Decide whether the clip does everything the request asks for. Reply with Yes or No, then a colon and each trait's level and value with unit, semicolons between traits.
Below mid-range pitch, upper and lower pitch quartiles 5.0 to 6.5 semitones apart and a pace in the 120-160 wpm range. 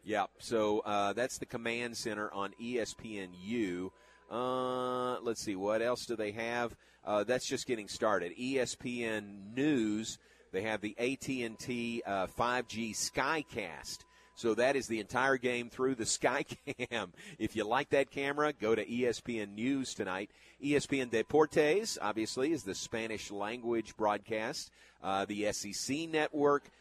No: low, 115 Hz; average, 3.2 semitones; average, 150 wpm